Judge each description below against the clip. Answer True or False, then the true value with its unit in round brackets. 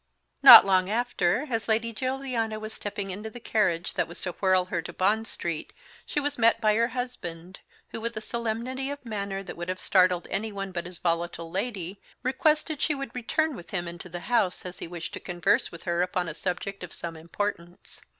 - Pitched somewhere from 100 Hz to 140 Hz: False (200 Hz)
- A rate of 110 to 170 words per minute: False (205 wpm)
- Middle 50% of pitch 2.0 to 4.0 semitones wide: False (4.7 semitones)